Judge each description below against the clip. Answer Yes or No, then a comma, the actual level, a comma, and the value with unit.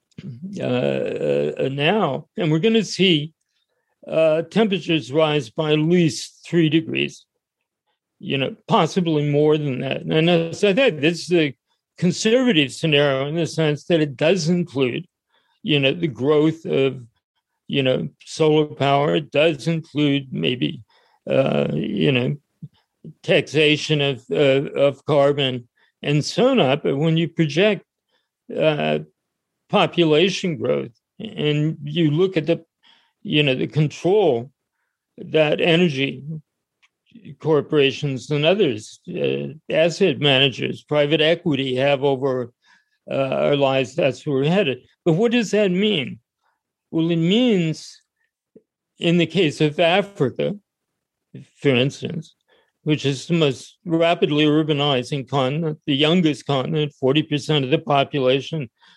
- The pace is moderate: No, slow, 130 wpm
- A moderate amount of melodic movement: Yes, average, 3.3 semitones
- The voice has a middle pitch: Yes, medium, 155 Hz